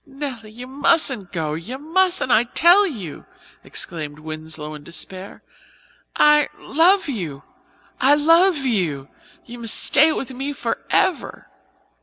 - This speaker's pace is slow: Yes, slow, 125 wpm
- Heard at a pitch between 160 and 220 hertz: No, very high, 250 Hz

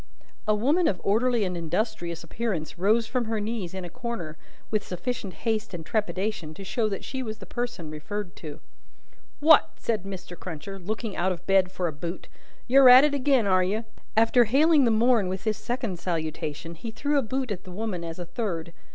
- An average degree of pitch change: Yes, average, 4.9 semitones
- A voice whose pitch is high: Yes, high, 205 Hz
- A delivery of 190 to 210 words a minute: Yes, average, 200 wpm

